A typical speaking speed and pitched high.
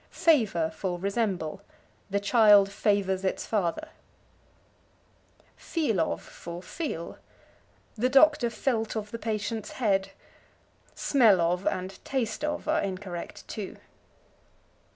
No: slow, 110 wpm; high, 205 Hz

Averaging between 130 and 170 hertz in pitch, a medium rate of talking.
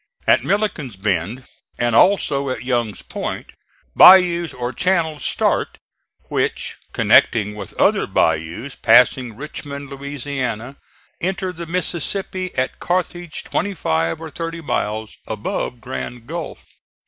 No: medium, 140 Hz; slow, 115 wpm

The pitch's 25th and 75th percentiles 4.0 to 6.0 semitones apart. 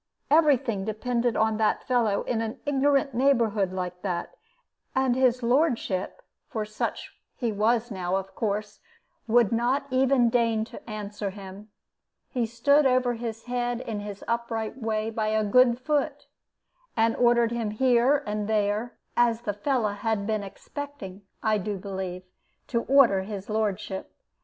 No: average, 3.0 semitones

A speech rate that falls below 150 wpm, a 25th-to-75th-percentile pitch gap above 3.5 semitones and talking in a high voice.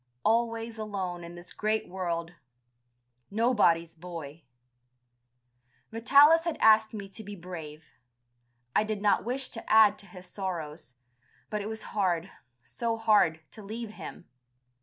Yes: slow, 135 wpm; average, 4.2 semitones; high, 205 Hz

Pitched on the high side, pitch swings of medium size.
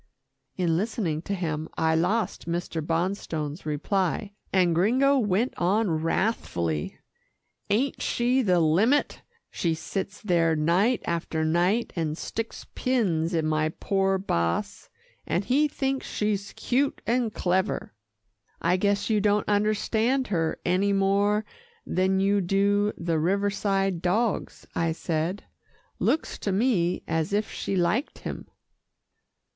Yes: high, 195 Hz; average, 4.1 semitones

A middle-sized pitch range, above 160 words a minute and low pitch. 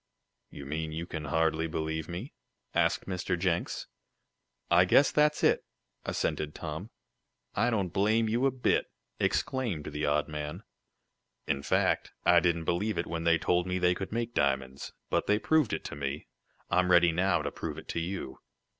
Yes: average, 3.9 semitones; average, 170 wpm; very low, 85 Hz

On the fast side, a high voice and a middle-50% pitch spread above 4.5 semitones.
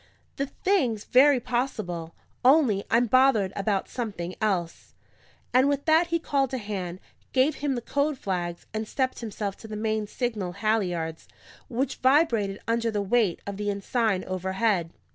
No: average, 155 wpm; high, 220 Hz; average, 4.9 semitones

